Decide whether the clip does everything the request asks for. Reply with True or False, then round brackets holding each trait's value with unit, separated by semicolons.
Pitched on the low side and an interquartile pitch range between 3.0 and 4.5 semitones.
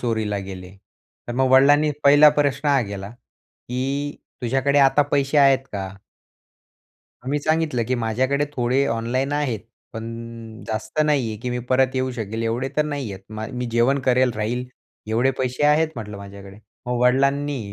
True (125 Hz; 3.7 semitones)